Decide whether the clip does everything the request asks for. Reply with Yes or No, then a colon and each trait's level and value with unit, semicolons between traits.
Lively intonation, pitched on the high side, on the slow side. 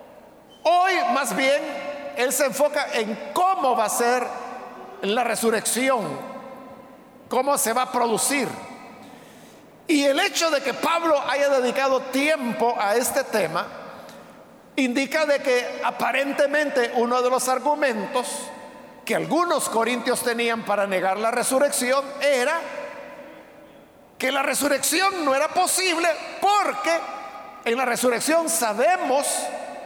No: average, 3.2 semitones; very high, 270 Hz; slow, 115 wpm